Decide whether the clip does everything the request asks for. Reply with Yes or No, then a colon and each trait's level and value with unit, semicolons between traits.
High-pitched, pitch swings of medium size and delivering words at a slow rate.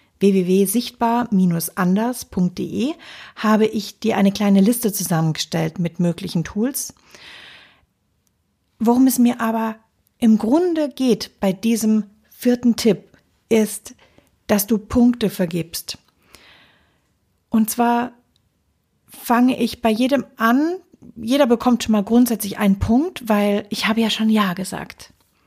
Yes: high, 220 Hz; average, 3.3 semitones; slow, 115 wpm